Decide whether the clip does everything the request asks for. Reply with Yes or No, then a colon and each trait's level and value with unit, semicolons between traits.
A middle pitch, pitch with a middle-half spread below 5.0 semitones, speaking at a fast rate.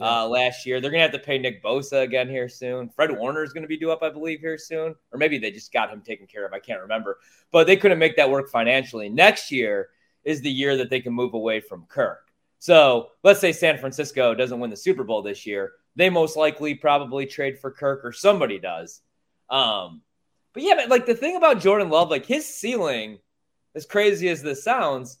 No: medium, 145 Hz; wide, 5.6 semitones; fast, 230 wpm